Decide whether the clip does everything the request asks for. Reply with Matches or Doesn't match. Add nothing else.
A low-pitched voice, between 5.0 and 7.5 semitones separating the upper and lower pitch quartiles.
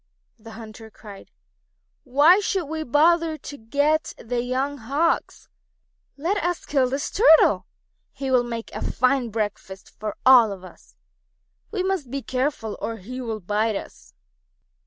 Doesn't match